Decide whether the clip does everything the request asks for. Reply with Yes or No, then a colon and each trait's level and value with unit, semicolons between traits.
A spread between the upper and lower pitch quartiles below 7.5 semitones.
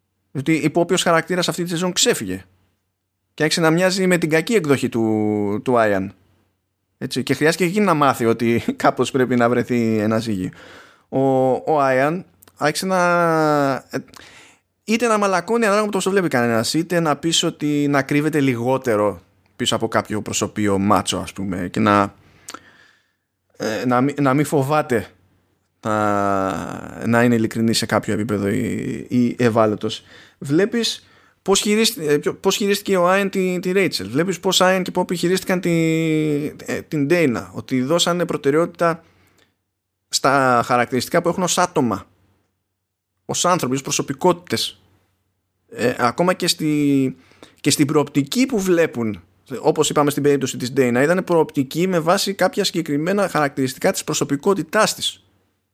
No: wide, 8.3 semitones